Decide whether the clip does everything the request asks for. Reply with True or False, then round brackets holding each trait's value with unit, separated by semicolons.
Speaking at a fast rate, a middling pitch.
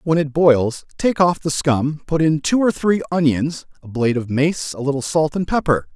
True (220 wpm; 150 Hz)